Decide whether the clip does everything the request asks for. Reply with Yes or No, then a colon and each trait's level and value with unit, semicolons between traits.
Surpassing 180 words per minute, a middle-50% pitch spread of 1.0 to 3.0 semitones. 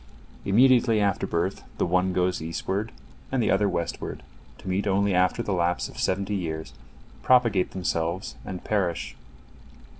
No: average, 145 wpm; narrow, 2.6 semitones